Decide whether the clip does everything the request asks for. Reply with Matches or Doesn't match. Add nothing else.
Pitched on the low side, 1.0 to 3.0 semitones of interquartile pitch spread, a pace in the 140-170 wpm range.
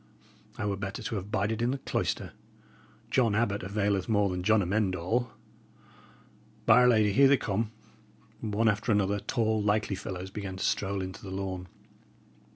Matches